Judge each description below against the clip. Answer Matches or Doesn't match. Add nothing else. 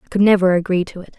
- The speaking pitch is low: Doesn't match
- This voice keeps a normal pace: Doesn't match